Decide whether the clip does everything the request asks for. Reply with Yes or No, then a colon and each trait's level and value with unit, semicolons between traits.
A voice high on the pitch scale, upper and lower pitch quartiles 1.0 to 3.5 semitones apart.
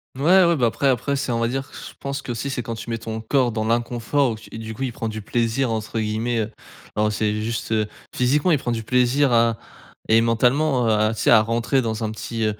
No: low, 115 Hz; average, 2.8 semitones